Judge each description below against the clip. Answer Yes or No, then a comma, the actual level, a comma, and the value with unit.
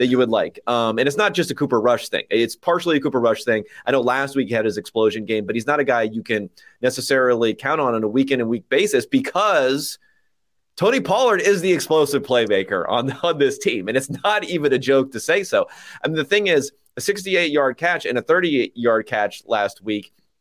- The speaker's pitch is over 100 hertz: Yes, low, 135 Hz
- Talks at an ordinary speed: No, fast, 235 wpm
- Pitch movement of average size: No, wide, 6.7 semitones